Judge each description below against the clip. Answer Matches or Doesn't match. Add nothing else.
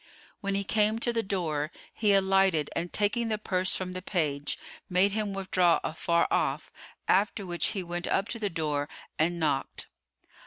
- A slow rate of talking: Doesn't match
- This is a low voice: Doesn't match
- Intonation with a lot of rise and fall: Doesn't match